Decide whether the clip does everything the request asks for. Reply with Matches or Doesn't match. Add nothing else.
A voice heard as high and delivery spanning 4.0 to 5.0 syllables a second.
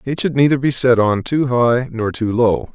Doesn't match